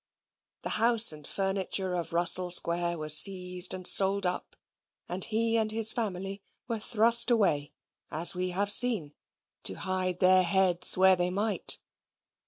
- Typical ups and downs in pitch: Yes, average, 3.0 semitones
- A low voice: No, medium, 185 Hz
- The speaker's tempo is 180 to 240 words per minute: No, average, 150 wpm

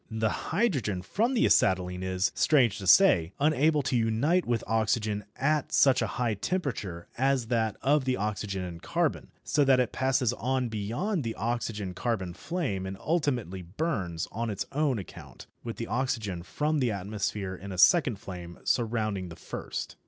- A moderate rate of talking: Yes, average, 165 wpm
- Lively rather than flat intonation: Yes, wide, 5.8 semitones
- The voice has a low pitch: Yes, low, 115 Hz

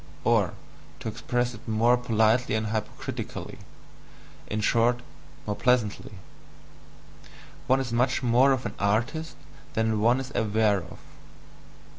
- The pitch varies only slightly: Yes, narrow, 2.3 semitones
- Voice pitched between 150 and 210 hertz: No, low, 115 Hz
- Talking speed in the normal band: No, slow, 120 wpm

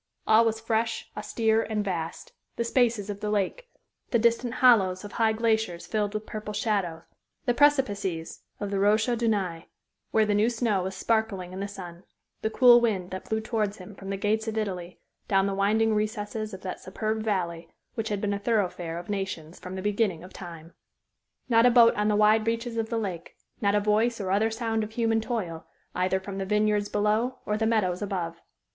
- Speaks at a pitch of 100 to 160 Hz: No, high, 210 Hz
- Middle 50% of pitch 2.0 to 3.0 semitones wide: Yes, average, 2.7 semitones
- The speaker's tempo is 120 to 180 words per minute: No, average, 200 wpm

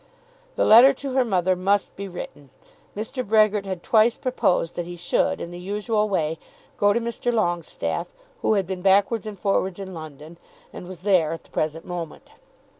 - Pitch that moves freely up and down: No, average, 3.7 semitones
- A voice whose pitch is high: Yes, high, 195 Hz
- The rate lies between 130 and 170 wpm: No, average, 185 wpm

